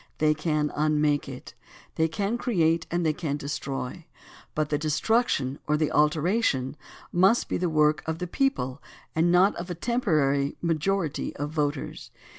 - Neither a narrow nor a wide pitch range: Yes, average, 3.1 semitones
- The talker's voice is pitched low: No, medium, 155 Hz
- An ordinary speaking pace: Yes, average, 155 wpm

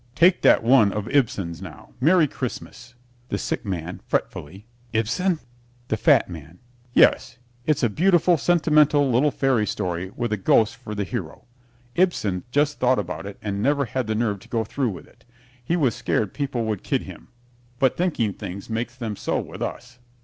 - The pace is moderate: Yes, average, 180 wpm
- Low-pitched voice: Yes, low, 120 Hz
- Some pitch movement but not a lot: No, wide, 5.7 semitones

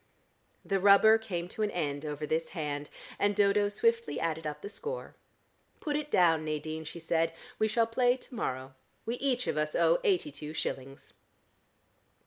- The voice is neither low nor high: Yes, medium, 180 Hz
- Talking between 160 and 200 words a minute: Yes, average, 170 wpm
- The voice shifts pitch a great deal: Yes, wide, 6.9 semitones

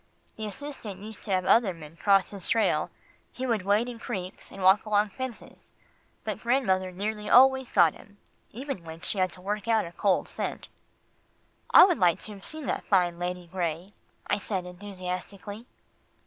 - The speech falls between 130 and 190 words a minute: Yes, average, 175 wpm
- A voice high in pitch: Yes, high, 200 Hz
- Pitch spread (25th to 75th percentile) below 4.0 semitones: Yes, average, 3.6 semitones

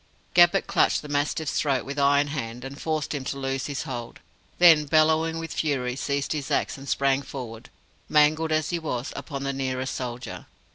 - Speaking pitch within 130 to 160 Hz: Yes, medium, 140 Hz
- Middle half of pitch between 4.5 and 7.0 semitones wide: No, average, 2.7 semitones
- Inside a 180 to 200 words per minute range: Yes, average, 185 wpm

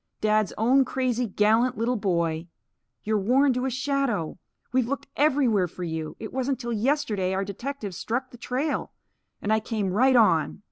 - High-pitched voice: Yes, high, 230 Hz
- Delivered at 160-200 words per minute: Yes, average, 170 wpm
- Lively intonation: No, average, 4.5 semitones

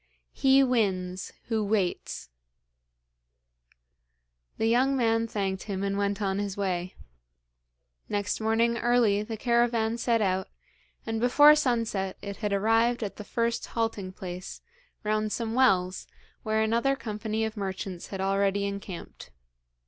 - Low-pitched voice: No, high, 215 Hz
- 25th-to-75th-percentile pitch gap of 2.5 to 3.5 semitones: Yes, average, 2.9 semitones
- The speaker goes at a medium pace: No, slow, 130 wpm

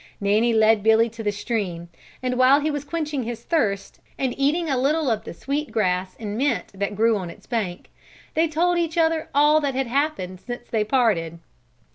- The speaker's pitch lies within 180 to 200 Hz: No, high, 240 Hz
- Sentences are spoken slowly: No, average, 195 wpm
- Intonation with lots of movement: Yes, wide, 5.8 semitones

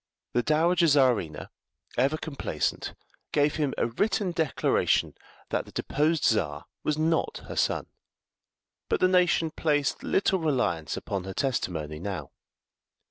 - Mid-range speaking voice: Yes, medium, 145 Hz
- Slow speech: Yes, slow, 130 wpm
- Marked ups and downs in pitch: Yes, wide, 7.6 semitones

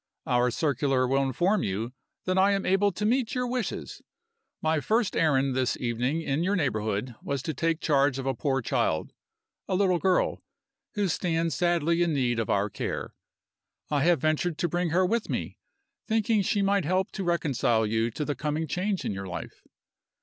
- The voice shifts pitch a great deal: Yes, wide, 6.2 semitones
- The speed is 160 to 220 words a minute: Yes, average, 185 wpm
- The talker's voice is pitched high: No, medium, 160 Hz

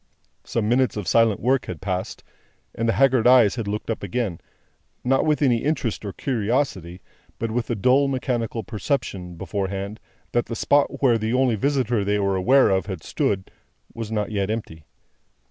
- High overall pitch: No, low, 115 Hz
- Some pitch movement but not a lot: Yes, average, 4.2 semitones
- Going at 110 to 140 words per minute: No, average, 175 wpm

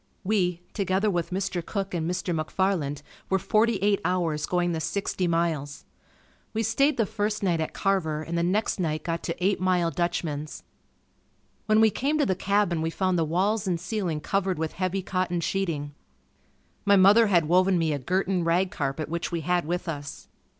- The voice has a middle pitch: Yes, medium, 180 Hz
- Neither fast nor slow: Yes, average, 185 wpm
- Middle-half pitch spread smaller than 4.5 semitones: Yes, average, 3.0 semitones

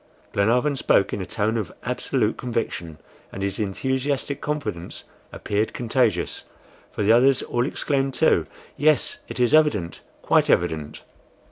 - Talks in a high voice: No, low, 115 Hz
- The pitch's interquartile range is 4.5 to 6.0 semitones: Yes, average, 5.3 semitones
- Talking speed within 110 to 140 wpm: Yes, slow, 135 wpm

